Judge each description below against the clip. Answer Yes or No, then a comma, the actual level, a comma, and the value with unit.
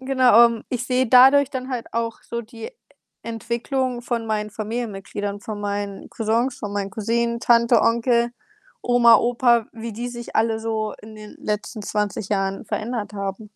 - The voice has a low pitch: No, high, 230 Hz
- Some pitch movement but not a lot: No, narrow, 2.2 semitones